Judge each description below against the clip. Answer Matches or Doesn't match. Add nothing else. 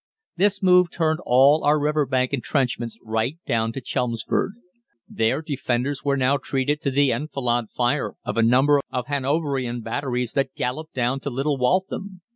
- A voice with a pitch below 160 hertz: Matches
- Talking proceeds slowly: Doesn't match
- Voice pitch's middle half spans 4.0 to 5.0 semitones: Doesn't match